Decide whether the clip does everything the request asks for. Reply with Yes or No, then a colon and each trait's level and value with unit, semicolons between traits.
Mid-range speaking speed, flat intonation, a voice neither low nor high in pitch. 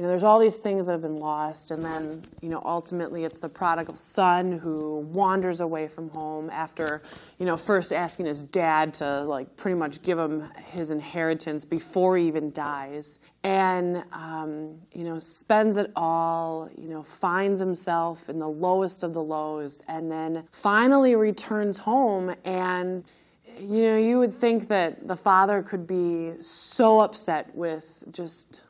No: average, 165 wpm; average, 3.0 semitones; medium, 170 Hz